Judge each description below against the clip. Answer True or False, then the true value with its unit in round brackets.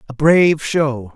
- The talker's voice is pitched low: False (145 Hz)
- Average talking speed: True (155 wpm)